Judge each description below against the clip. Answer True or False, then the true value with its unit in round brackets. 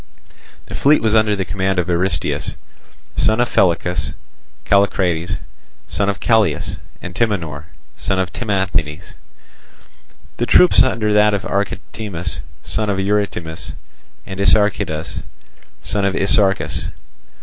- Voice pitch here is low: True (100 Hz)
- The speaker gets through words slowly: True (115 wpm)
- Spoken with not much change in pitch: False (3.0 semitones)